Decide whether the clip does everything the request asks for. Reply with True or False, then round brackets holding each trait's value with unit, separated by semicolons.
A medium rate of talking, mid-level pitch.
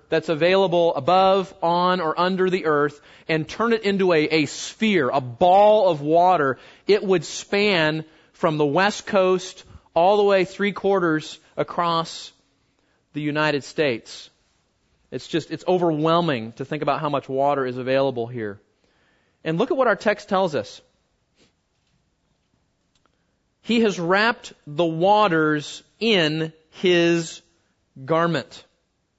False (130 wpm; 170 Hz)